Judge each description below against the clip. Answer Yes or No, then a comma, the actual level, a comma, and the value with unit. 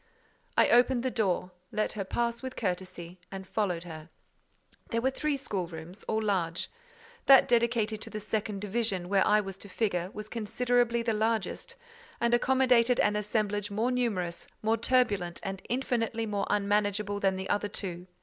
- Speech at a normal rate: Yes, average, 160 wpm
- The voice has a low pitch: No, high, 210 Hz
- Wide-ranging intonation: No, average, 3.6 semitones